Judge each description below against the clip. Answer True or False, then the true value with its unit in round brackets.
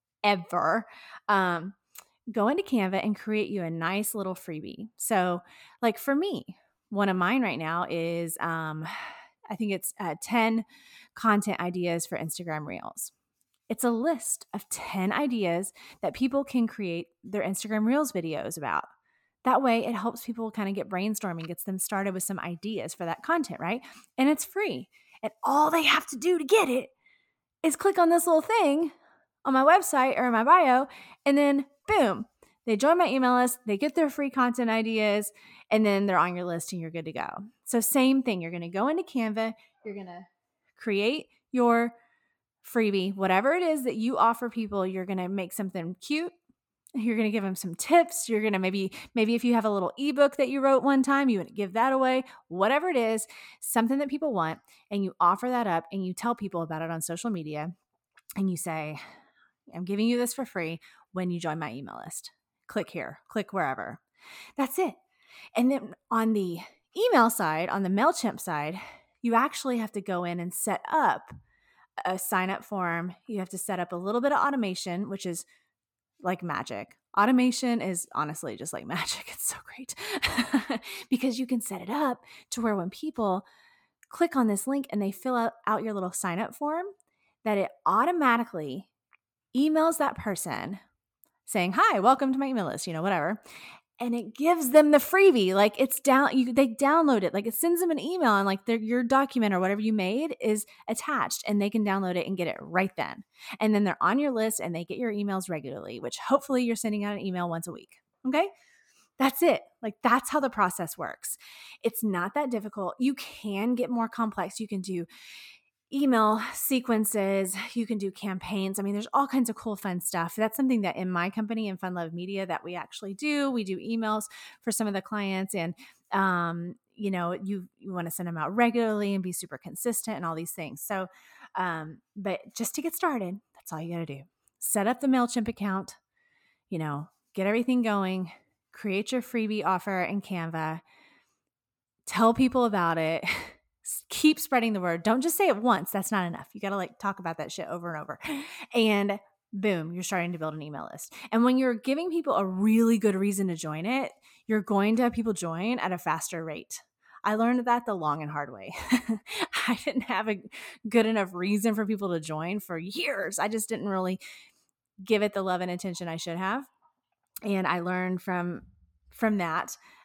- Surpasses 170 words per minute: True (200 wpm)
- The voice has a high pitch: True (215 Hz)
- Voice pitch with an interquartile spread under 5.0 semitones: False (5.4 semitones)